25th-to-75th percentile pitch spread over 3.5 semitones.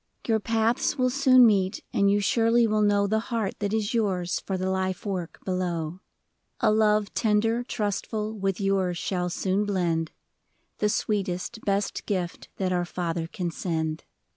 No: average, 3.2 semitones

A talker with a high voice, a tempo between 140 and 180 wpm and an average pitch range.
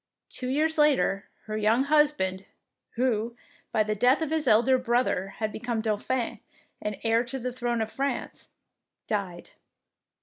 Yes: high, 235 Hz; average, 145 wpm; average, 3.5 semitones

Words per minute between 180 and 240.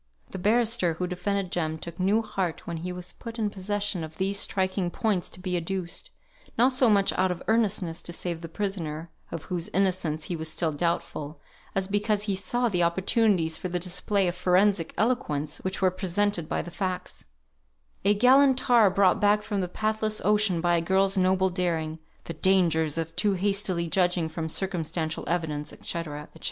Yes: average, 185 wpm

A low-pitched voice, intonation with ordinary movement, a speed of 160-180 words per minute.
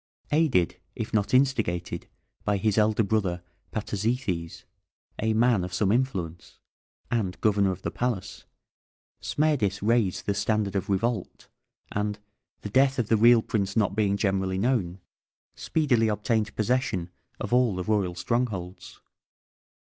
No: low, 105 Hz; average, 3.7 semitones; slow, 135 wpm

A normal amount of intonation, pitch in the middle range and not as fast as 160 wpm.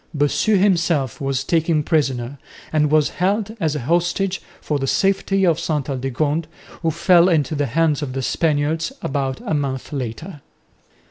Yes: average, 3.7 semitones; medium, 150 Hz; average, 150 wpm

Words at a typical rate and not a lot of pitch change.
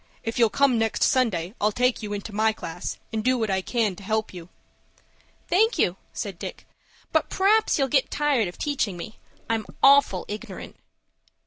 No: average, 180 wpm; average, 4.6 semitones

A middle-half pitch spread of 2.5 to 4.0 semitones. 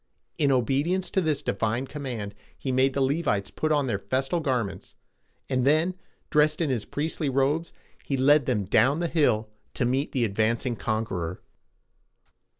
No: average, 4.6 semitones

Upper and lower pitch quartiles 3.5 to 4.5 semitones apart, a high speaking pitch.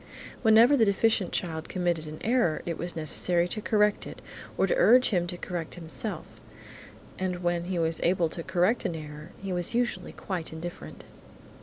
No: average, 4.0 semitones; medium, 175 Hz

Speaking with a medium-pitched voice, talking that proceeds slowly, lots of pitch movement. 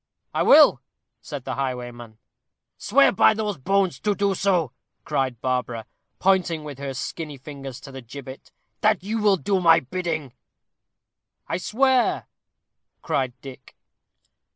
Yes: medium, 150 Hz; slow, 130 wpm; wide, 6.9 semitones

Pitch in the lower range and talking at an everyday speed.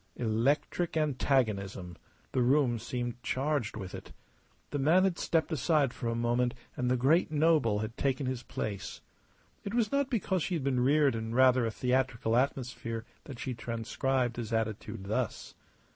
Yes: low, 125 Hz; average, 160 wpm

